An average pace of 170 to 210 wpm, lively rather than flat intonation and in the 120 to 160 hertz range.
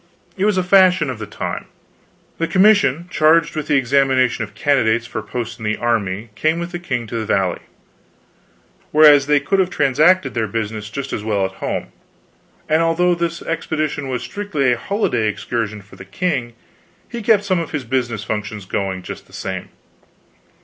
Yes: average, 180 wpm; wide, 7.2 semitones; low, 135 Hz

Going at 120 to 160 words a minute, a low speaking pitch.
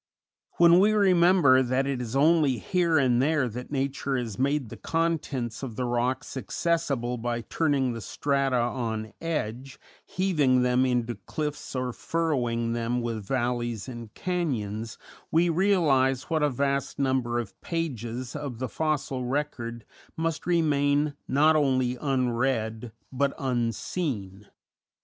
Yes: slow, 135 wpm; low, 130 Hz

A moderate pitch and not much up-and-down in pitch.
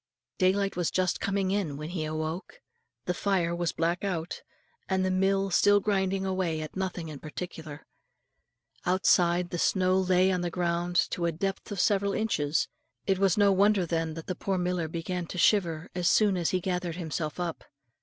Yes: medium, 180 Hz; narrow, 2.3 semitones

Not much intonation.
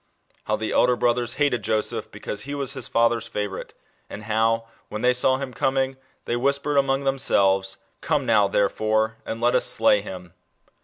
No: average, 3.7 semitones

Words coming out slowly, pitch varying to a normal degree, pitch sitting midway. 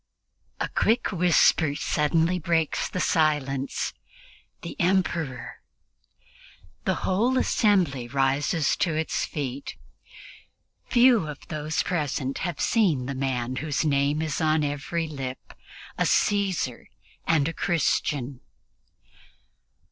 Yes: slow, 110 wpm; average, 3.8 semitones; medium, 155 Hz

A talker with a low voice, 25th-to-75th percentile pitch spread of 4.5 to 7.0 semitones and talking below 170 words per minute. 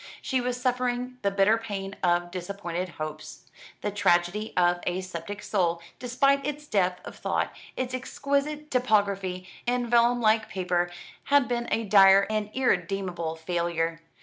No: high, 200 Hz; wide, 5.6 semitones; average, 145 wpm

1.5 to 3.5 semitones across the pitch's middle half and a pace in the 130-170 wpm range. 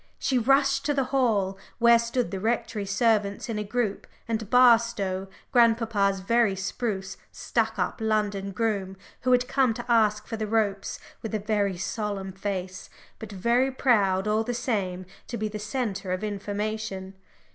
Yes: average, 3.1 semitones; average, 160 wpm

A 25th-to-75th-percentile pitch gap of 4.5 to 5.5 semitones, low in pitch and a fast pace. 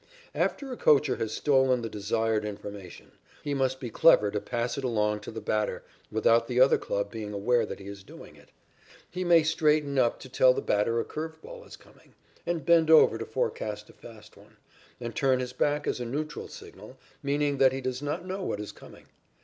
Yes: average, 5.2 semitones; low, 130 Hz; fast, 210 wpm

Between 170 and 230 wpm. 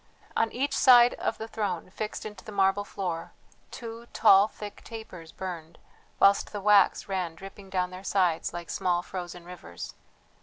No: average, 160 wpm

